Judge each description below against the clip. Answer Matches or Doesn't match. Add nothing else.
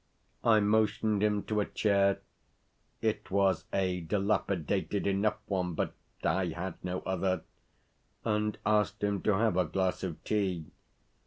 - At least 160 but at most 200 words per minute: Doesn't match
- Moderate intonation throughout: Doesn't match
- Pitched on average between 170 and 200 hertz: Doesn't match